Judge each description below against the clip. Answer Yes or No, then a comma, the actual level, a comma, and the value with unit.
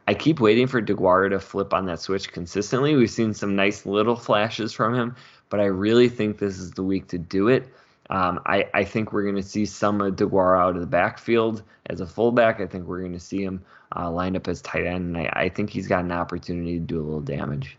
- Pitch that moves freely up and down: No, average, 2.9 semitones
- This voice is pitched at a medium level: No, very low, 95 Hz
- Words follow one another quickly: Yes, fast, 250 wpm